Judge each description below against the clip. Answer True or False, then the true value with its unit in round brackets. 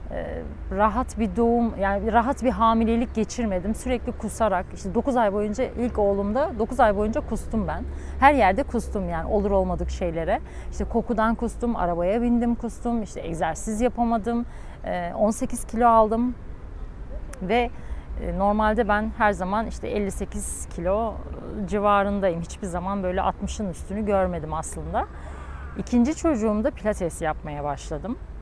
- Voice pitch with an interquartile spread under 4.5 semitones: True (3.4 semitones)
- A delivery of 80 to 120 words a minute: False (130 wpm)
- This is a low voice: False (215 Hz)